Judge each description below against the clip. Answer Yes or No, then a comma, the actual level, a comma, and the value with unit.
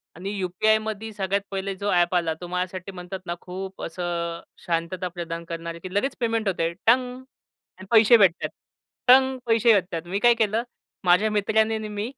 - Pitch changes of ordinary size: Yes, average, 3.7 semitones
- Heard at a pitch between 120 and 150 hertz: No, high, 195 Hz